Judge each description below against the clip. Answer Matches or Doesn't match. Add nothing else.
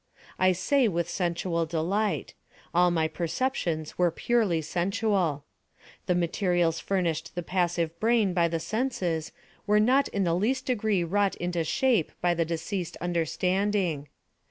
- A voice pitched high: Doesn't match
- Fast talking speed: Doesn't match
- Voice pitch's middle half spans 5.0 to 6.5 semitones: Doesn't match